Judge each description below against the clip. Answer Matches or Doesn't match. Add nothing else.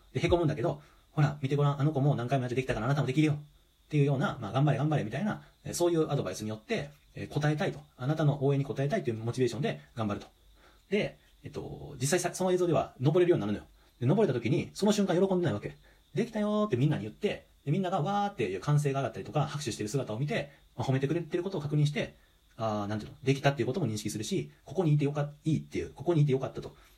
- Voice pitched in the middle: Matches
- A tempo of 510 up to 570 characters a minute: Matches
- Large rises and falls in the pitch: Doesn't match